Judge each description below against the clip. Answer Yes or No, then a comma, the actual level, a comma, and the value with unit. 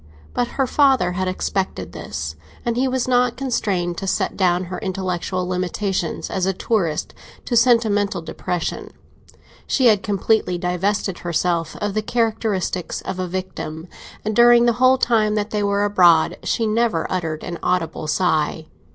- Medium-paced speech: Yes, average, 155 wpm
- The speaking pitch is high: Yes, high, 195 Hz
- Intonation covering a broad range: No, average, 4.1 semitones